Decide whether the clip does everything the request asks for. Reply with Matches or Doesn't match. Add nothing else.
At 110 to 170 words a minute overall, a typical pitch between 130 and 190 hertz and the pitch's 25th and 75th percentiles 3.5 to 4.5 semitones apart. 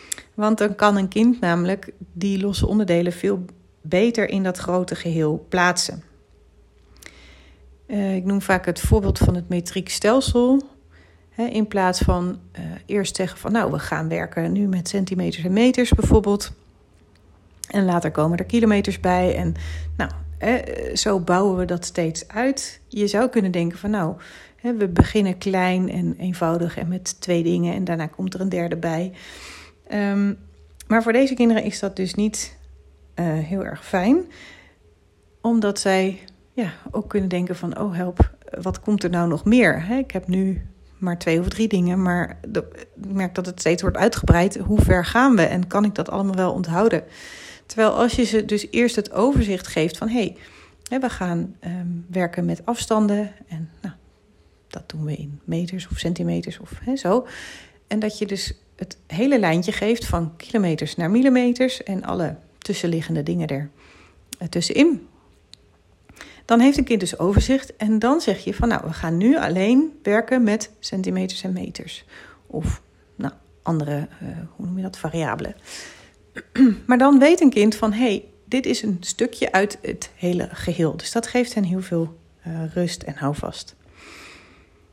Matches